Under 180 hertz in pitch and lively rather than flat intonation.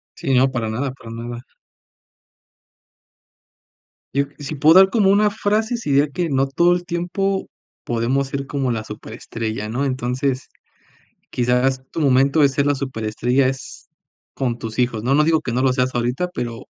No: low, 135 Hz; average, 3.8 semitones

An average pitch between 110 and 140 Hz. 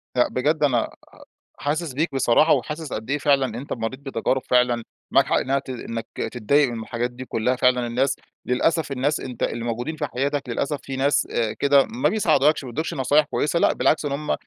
Yes: low, 135 Hz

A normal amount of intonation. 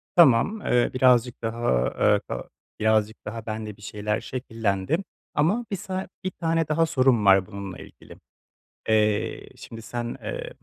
No: wide, 6.5 semitones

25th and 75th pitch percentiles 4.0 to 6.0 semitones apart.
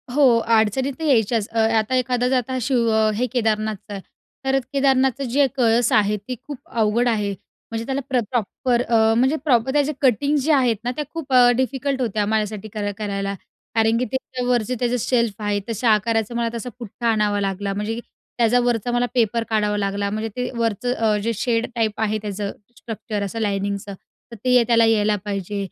No: average, 3.0 semitones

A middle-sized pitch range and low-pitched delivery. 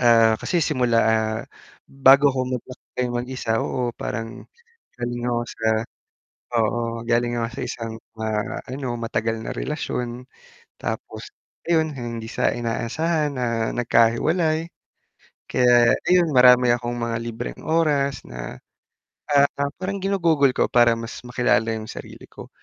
Yes: average, 3.4 semitones; low, 120 Hz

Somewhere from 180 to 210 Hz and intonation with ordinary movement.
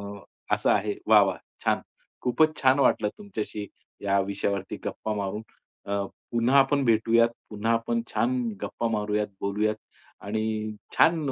No: low, 110 Hz; average, 3.7 semitones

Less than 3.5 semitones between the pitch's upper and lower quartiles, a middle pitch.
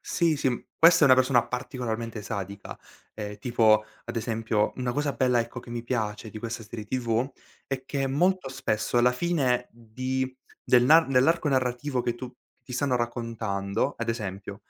No: narrow, 2.6 semitones; low, 120 Hz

